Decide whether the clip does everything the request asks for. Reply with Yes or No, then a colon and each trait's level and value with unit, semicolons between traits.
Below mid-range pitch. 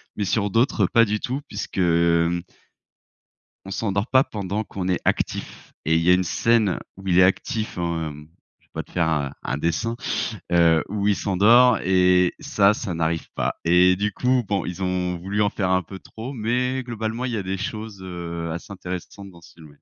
Yes: very low, 95 Hz